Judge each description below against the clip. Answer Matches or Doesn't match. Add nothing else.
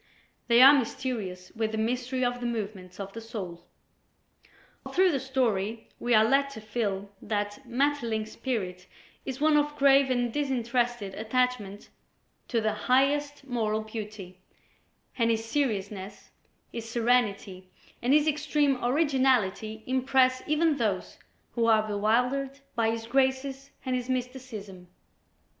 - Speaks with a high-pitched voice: Matches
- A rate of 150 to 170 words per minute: Doesn't match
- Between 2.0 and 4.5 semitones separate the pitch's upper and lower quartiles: Matches